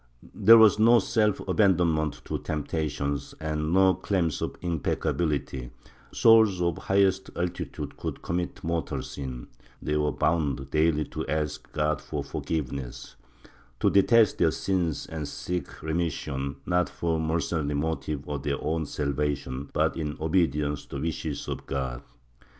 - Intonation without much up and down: No, average, 3.3 semitones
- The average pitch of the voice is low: Yes, very low, 80 Hz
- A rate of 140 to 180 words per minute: Yes, average, 145 wpm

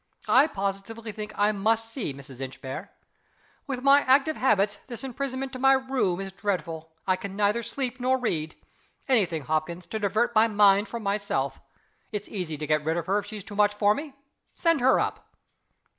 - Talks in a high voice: Yes, high, 210 Hz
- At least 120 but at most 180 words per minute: No, average, 190 wpm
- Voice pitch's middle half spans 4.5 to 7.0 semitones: Yes, average, 5.2 semitones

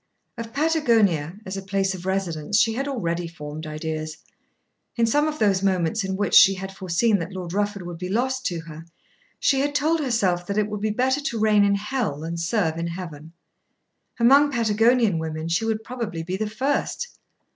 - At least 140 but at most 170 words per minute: No, average, 190 wpm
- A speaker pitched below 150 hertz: No, high, 200 Hz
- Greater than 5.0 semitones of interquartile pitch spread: Yes, wide, 5.5 semitones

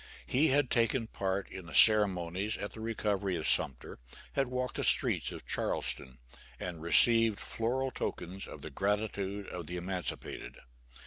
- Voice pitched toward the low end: Yes, low, 100 Hz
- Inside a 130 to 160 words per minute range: Yes, average, 150 wpm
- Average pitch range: Yes, average, 4.1 semitones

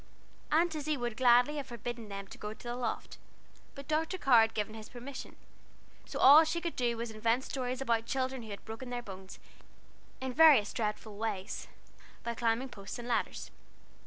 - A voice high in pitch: Yes, high, 240 Hz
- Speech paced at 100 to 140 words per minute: No, average, 185 wpm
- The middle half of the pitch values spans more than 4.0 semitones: No, average, 3.3 semitones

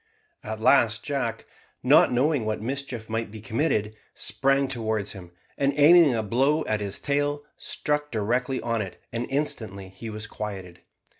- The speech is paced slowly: No, average, 155 wpm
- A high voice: No, low, 115 Hz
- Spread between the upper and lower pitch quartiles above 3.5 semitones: Yes, average, 4.5 semitones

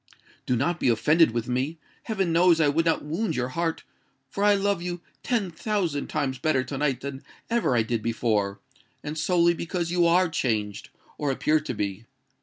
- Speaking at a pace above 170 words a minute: Yes, average, 180 wpm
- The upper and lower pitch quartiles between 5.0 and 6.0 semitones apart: Yes, wide, 5.6 semitones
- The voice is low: No, medium, 150 Hz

